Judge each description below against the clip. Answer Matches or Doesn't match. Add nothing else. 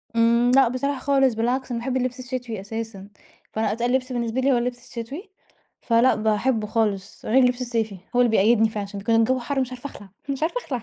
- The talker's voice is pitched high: Matches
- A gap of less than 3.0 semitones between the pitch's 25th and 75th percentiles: Matches